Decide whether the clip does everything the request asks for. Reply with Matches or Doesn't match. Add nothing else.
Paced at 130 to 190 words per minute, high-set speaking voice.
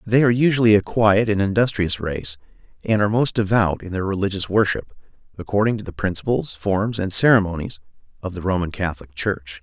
Doesn't match